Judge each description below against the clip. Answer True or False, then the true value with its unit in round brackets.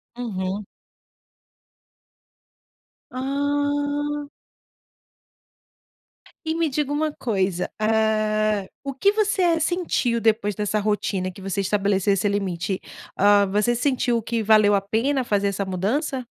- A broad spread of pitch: True (6.1 semitones)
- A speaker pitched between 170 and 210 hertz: False (220 Hz)